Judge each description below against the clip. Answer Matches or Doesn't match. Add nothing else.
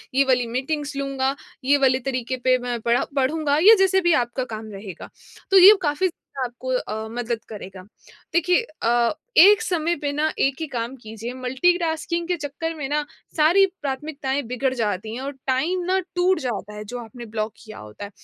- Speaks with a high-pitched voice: Matches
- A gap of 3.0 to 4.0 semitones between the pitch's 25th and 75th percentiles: Doesn't match